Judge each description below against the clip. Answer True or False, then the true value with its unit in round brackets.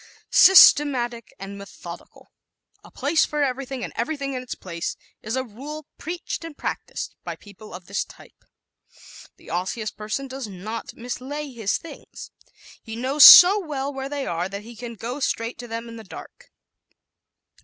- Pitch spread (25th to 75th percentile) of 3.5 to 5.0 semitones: True (4.6 semitones)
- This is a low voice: False (245 Hz)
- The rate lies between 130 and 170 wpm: True (165 wpm)